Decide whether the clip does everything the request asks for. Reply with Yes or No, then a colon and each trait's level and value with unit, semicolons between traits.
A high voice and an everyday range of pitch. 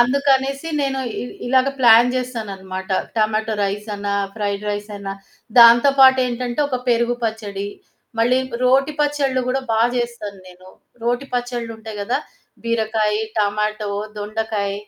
Yes: high, 230 Hz; average, 3.3 semitones